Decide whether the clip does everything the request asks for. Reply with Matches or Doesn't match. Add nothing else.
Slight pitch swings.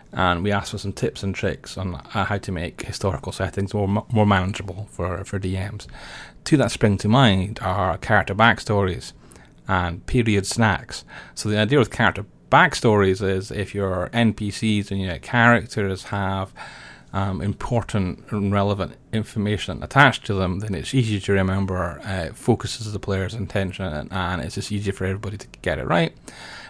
Matches